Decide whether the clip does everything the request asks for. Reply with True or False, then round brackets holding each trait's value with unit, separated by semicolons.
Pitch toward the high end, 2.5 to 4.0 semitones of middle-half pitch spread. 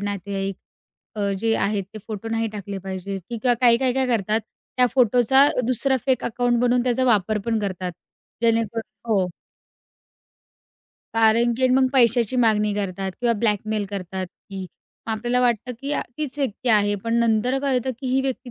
True (225 Hz; 3.5 semitones)